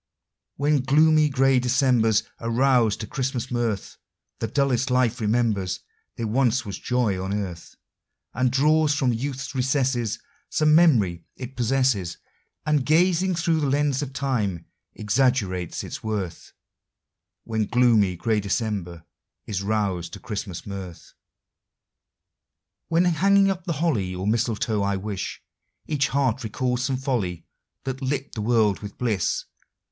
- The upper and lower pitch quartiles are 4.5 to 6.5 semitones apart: Yes, average, 4.8 semitones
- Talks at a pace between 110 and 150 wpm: Yes, slow, 135 wpm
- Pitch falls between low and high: No, low, 120 Hz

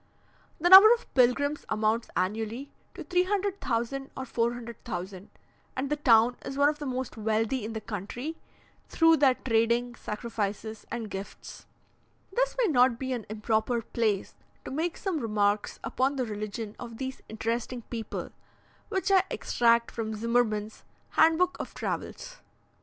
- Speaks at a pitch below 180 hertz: No, high, 235 Hz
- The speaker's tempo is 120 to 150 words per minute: Yes, average, 140 wpm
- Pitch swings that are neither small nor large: Yes, average, 4.3 semitones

